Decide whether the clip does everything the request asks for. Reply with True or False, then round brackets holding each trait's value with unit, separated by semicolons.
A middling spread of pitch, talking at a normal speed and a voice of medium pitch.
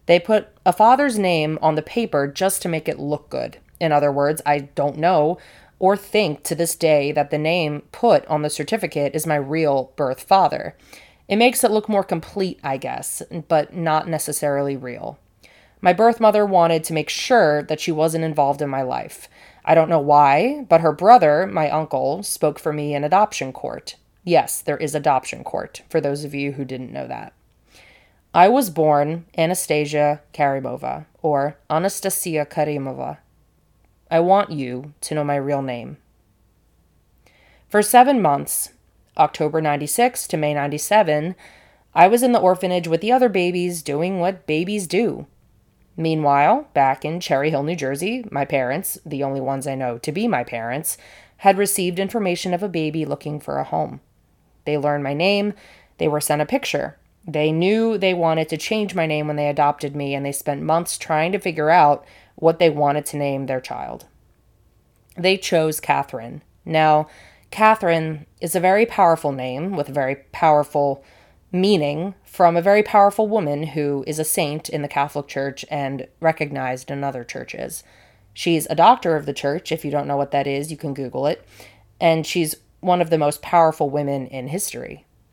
True (4.1 semitones; 175 wpm; 155 Hz)